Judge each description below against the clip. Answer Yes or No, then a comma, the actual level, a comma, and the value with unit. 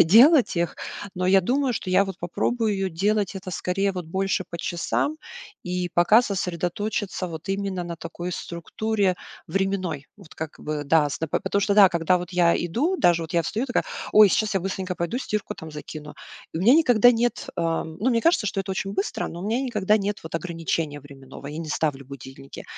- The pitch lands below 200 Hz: Yes, medium, 185 Hz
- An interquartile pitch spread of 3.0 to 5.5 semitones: Yes, average, 4.0 semitones